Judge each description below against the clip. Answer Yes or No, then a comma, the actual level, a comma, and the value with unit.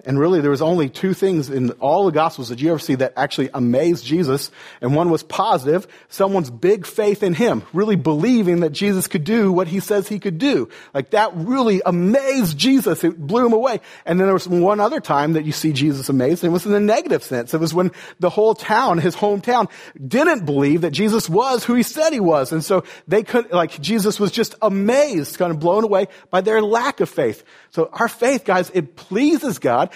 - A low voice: No, medium, 185 Hz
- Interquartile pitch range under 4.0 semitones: No, average, 5.0 semitones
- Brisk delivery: Yes, fast, 220 wpm